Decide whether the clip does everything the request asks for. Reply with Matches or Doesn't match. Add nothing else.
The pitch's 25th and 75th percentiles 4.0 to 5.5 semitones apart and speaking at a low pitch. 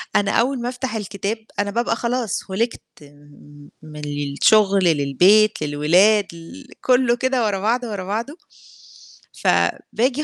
Doesn't match